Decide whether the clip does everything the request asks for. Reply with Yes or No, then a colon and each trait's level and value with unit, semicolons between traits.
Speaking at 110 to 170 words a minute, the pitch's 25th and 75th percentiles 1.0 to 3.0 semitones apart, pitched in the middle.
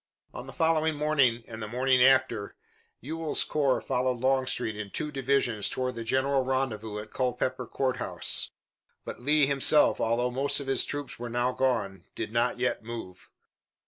No: average, 165 wpm; average, 2.7 semitones; low, 130 Hz